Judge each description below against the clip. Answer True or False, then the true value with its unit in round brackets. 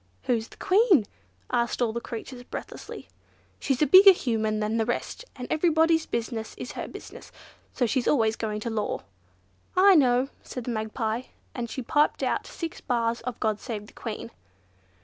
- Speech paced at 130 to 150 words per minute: False (170 wpm)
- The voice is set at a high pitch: True (240 Hz)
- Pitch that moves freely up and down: False (4.2 semitones)